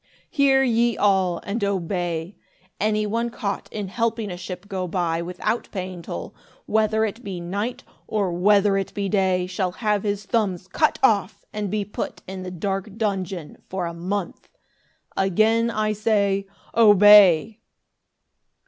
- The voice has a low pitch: No, high, 200 Hz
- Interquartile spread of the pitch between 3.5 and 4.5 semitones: No, average, 2.7 semitones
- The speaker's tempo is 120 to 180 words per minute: Yes, average, 150 wpm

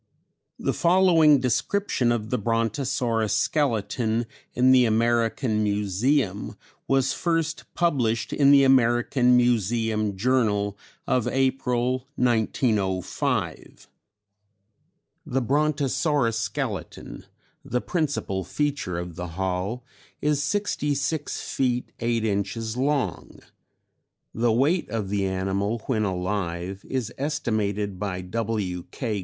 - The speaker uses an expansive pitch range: No, average, 4.6 semitones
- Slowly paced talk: Yes, slow, 100 wpm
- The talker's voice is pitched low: Yes, low, 120 Hz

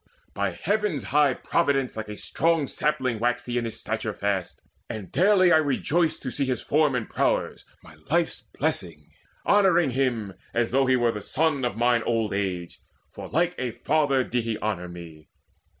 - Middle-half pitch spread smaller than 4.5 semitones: No, wide, 5.6 semitones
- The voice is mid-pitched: No, low, 125 Hz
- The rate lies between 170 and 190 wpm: Yes, average, 175 wpm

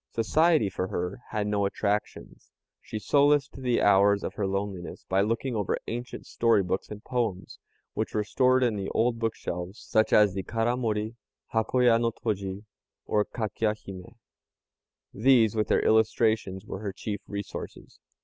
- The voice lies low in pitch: Yes, low, 110 Hz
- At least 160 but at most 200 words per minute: No, average, 150 wpm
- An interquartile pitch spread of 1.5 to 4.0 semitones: Yes, average, 2.7 semitones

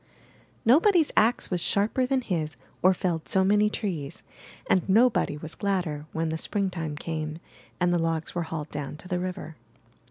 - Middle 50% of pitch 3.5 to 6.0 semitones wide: Yes, average, 4.4 semitones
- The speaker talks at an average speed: Yes, average, 165 wpm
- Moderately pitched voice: Yes, medium, 180 Hz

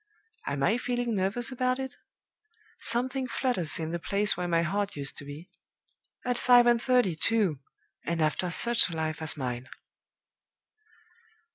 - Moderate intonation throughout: No, wide, 7.3 semitones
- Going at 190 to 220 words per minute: No, average, 150 wpm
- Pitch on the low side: No, high, 200 Hz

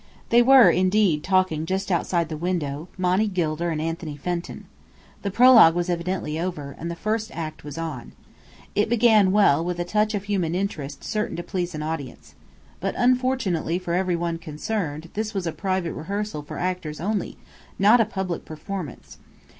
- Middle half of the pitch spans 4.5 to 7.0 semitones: No, average, 3.9 semitones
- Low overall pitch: No, medium, 180 Hz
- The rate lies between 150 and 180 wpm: Yes, average, 170 wpm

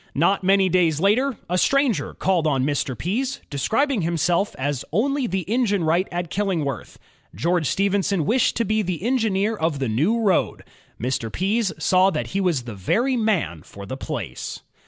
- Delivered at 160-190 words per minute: Yes, average, 170 wpm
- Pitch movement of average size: No, wide, 6.4 semitones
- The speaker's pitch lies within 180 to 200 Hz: Yes, medium, 185 Hz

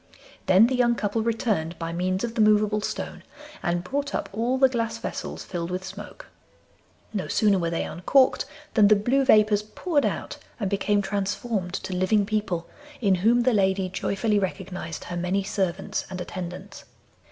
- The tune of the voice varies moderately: Yes, average, 3.5 semitones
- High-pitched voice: Yes, high, 200 Hz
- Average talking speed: Yes, average, 170 wpm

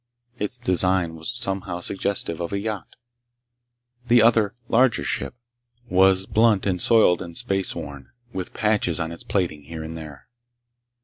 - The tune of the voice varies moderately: Yes, average, 4.0 semitones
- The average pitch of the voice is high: No, very low, 95 Hz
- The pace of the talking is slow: No, average, 145 wpm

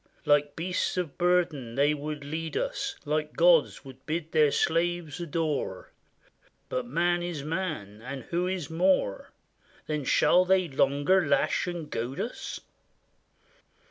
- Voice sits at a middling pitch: Yes, medium, 155 Hz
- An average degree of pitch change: Yes, average, 3.7 semitones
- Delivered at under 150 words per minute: Yes, slow, 135 wpm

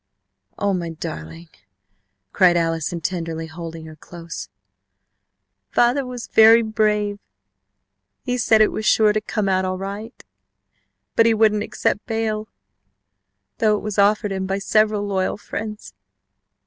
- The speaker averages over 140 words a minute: No, slow, 135 wpm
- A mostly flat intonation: No, average, 3.7 semitones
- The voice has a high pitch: Yes, high, 205 Hz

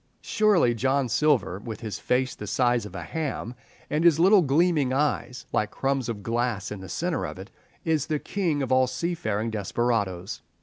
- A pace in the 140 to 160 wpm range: No, average, 180 wpm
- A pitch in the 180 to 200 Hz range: No, low, 125 Hz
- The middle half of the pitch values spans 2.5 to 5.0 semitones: No, wide, 5.5 semitones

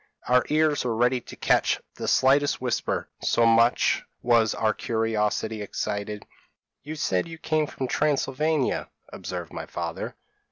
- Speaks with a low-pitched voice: Yes, low, 125 Hz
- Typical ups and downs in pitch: Yes, average, 4.5 semitones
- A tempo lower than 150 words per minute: Yes, slow, 135 wpm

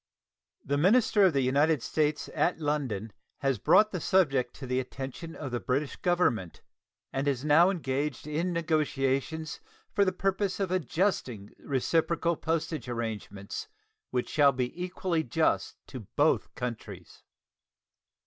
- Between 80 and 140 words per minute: Yes, slow, 135 wpm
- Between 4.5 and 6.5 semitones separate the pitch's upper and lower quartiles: Yes, average, 4.9 semitones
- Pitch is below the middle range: No, medium, 150 Hz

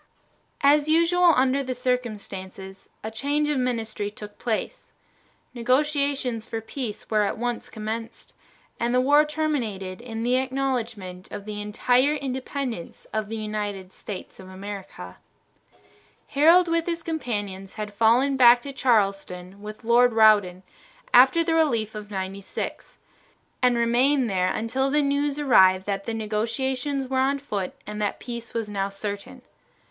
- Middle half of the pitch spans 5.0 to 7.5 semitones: No, average, 4.6 semitones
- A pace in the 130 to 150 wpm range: Yes, average, 145 wpm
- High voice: Yes, high, 235 Hz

